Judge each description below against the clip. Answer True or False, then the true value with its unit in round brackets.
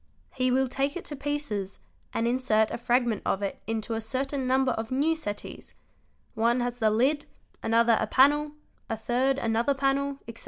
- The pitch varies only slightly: False (3.5 semitones)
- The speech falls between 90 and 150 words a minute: False (180 wpm)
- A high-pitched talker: True (250 Hz)